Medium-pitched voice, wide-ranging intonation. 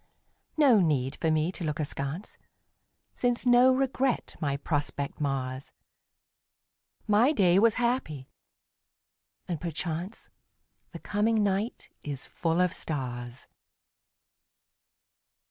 Yes: medium, 170 Hz; wide, 7.8 semitones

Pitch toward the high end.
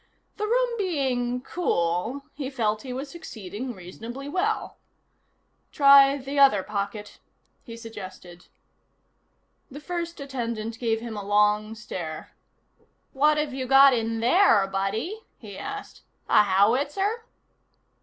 Yes: high, 245 Hz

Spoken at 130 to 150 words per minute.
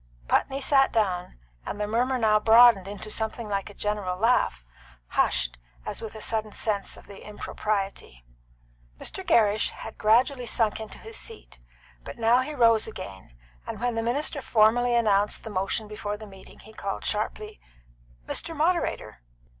No: average, 160 wpm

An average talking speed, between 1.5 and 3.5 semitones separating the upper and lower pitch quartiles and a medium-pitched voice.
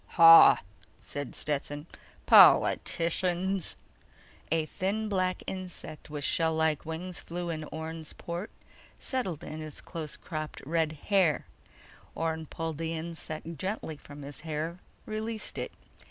No: slow, 125 wpm; average, 2.7 semitones; medium, 165 Hz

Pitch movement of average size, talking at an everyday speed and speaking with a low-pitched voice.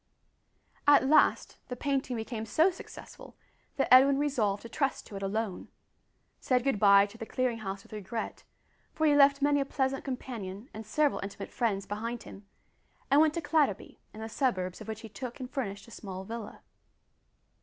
No: average, 4.9 semitones; average, 180 wpm; high, 235 Hz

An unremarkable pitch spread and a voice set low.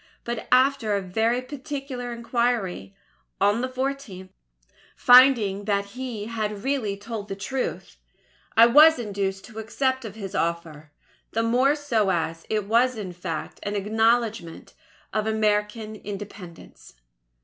No: average, 3.7 semitones; high, 220 Hz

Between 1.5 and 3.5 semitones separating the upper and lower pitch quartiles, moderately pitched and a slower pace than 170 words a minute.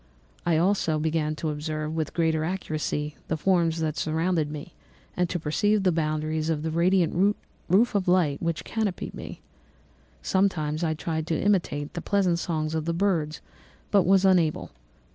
Yes: average, 3.0 semitones; medium, 165 Hz; average, 160 wpm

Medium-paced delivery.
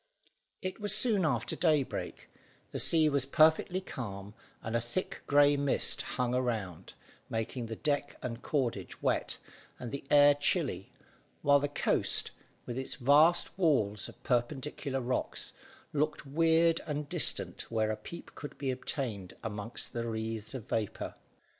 Yes: average, 145 wpm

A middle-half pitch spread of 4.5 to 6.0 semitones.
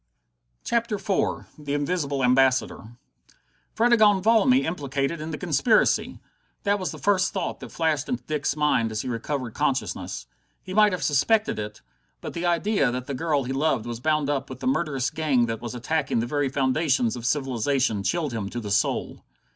Yes: wide, 5.5 semitones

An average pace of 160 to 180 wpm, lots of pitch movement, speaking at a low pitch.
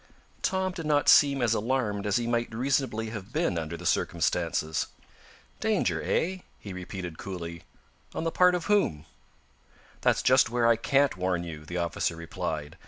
Yes: average, 165 wpm; wide, 7.9 semitones; low, 110 Hz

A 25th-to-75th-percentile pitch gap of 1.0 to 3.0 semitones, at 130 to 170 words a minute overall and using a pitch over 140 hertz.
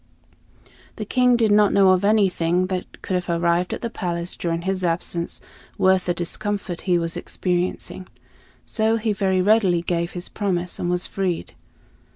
Yes: narrow, 2.6 semitones; average, 165 wpm; medium, 185 Hz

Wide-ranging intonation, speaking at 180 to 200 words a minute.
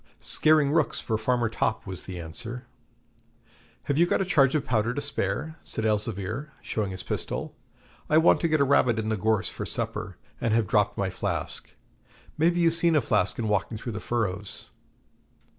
Yes: wide, 6.0 semitones; average, 185 wpm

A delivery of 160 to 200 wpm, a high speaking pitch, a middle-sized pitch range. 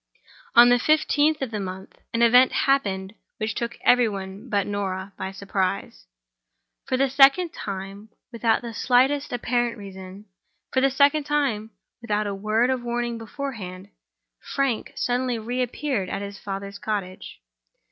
No: average, 140 wpm; high, 225 Hz; average, 4.4 semitones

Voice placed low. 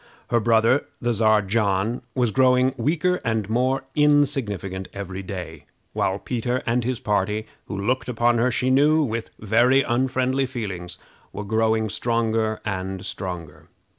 Yes: low, 115 Hz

